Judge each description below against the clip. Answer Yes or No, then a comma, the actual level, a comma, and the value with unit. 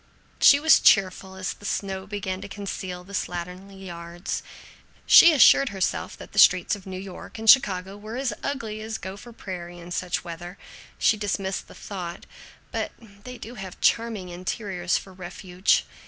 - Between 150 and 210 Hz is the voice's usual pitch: Yes, high, 190 Hz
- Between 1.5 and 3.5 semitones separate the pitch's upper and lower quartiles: Yes, average, 2.8 semitones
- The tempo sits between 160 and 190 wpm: Yes, average, 165 wpm